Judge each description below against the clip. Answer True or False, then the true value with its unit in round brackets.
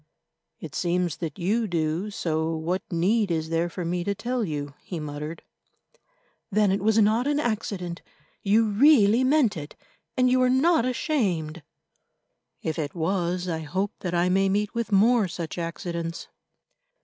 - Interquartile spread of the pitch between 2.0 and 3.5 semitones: False (4.9 semitones)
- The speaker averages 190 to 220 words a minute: False (160 wpm)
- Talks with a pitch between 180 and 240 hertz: True (185 Hz)